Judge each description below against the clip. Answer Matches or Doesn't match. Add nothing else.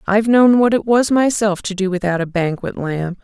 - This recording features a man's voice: Doesn't match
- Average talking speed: Doesn't match